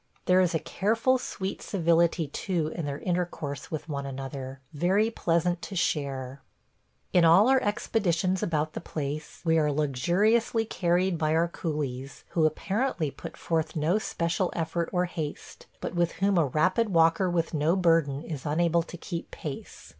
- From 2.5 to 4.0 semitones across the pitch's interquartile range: Yes, average, 3.2 semitones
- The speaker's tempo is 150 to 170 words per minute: Yes, average, 160 wpm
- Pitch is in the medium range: Yes, medium, 165 Hz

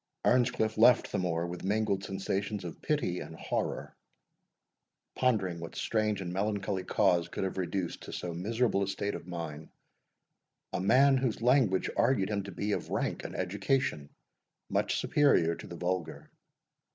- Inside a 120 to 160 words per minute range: Yes, average, 155 wpm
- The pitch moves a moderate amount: Yes, average, 3.8 semitones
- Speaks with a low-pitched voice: Yes, very low, 95 Hz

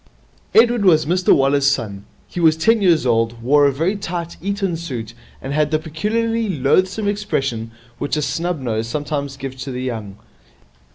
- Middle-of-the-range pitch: Yes, medium, 150 Hz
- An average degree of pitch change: No, wide, 6.0 semitones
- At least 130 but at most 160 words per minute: No, average, 170 wpm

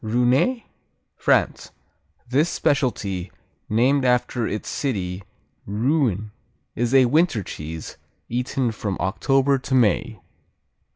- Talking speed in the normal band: No, slow, 100 wpm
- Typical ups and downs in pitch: Yes, average, 4.6 semitones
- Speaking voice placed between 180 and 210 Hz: No, low, 120 Hz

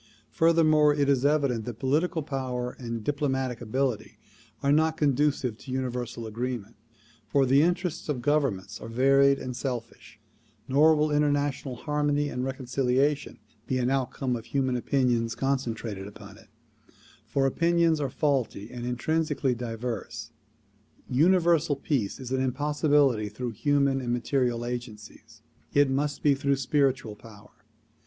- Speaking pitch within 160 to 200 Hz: No, low, 135 Hz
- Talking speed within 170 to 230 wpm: No, slow, 135 wpm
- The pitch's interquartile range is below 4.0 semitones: Yes, average, 3.2 semitones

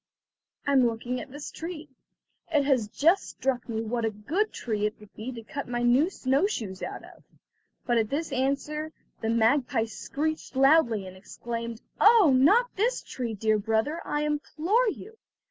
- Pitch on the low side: No, very high, 260 Hz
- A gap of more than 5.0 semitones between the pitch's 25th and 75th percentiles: Yes, wide, 5.4 semitones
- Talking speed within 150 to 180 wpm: Yes, average, 170 wpm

